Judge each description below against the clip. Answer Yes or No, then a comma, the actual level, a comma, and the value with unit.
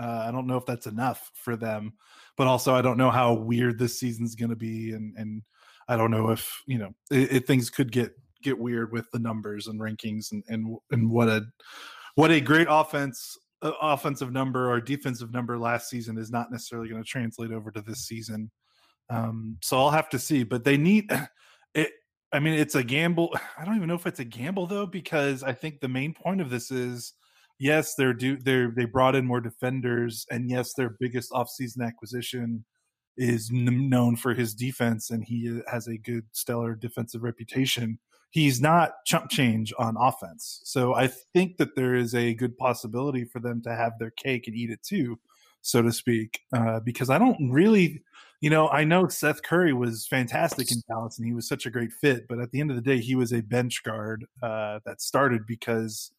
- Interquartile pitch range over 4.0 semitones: No, average, 2.8 semitones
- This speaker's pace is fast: Yes, fast, 210 wpm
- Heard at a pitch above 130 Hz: No, low, 125 Hz